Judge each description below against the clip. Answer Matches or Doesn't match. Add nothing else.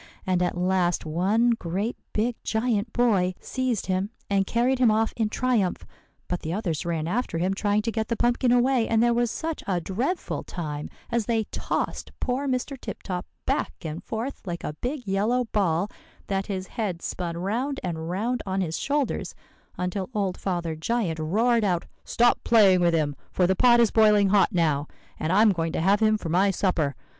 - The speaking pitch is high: Matches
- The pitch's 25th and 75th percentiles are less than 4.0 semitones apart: Doesn't match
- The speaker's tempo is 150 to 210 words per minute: Matches